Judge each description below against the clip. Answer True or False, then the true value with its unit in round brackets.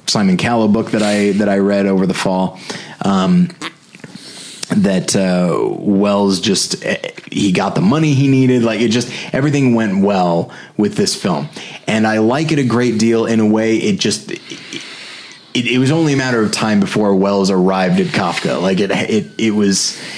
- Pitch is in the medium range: False (110 Hz)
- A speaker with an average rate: True (185 wpm)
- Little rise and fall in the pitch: False (3.7 semitones)